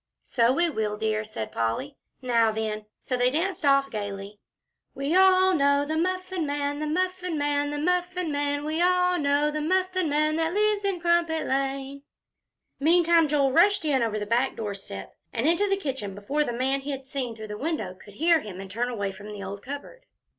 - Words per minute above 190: Yes, average, 200 wpm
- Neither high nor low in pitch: No, very high, 285 Hz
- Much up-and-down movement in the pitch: Yes, wide, 6.9 semitones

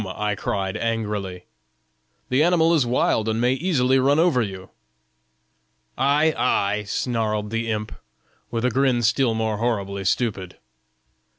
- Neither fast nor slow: No, slow, 130 wpm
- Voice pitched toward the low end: Yes, low, 115 Hz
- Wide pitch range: No, average, 3.9 semitones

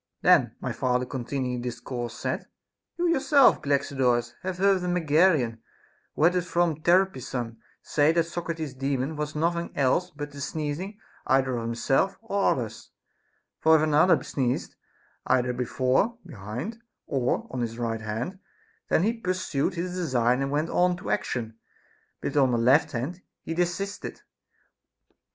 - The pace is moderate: Yes, average, 160 wpm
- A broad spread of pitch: Yes, wide, 6.1 semitones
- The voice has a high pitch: No, medium, 145 Hz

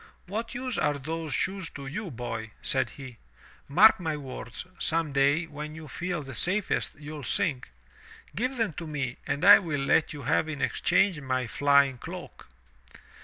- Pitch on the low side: No, medium, 150 Hz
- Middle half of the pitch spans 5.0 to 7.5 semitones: No, average, 4.3 semitones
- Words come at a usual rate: Yes, average, 170 wpm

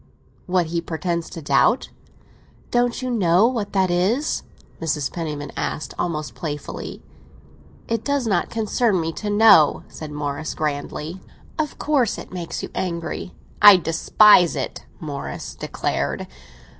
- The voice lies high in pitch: No, medium, 175 Hz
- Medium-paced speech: No, slow, 130 wpm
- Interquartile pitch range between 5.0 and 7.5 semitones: Yes, wide, 5.4 semitones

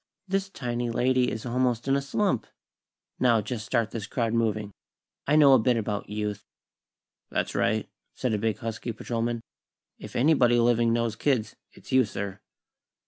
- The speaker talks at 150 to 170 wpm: Yes, average, 160 wpm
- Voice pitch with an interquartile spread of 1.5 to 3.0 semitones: Yes, narrow, 2.5 semitones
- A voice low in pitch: Yes, low, 120 Hz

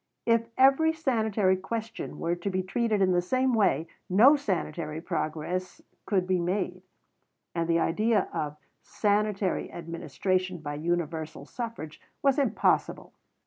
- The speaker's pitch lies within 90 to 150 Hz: No, medium, 185 Hz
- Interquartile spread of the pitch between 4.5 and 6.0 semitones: Yes, average, 5.0 semitones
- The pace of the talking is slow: Yes, slow, 130 wpm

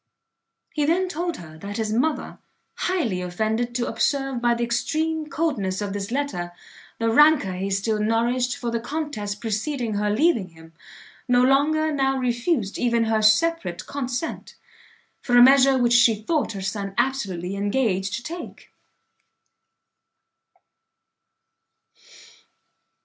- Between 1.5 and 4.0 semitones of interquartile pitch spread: No, wide, 5.5 semitones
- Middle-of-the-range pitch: No, high, 235 Hz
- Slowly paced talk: Yes, slow, 130 wpm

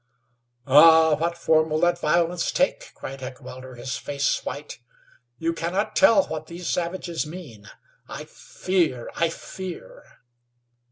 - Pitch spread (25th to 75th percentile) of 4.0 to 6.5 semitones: No, average, 3.4 semitones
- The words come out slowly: Yes, slow, 125 wpm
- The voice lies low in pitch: No, medium, 165 Hz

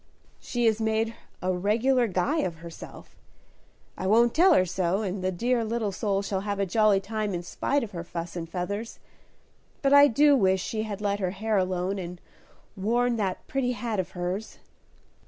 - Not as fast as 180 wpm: No, average, 185 wpm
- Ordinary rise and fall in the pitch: Yes, average, 3.7 semitones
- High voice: Yes, high, 205 Hz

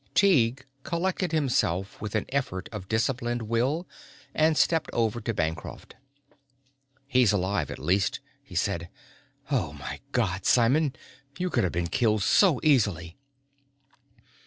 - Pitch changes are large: Yes, wide, 6.8 semitones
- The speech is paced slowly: Yes, slow, 130 wpm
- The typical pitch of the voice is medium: No, low, 120 Hz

